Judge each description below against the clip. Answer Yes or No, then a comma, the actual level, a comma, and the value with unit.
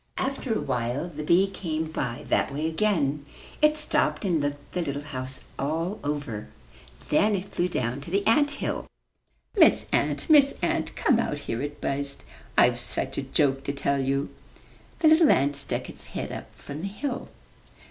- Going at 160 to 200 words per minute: Yes, average, 175 wpm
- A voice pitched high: No, medium, 150 Hz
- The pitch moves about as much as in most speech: No, wide, 6.2 semitones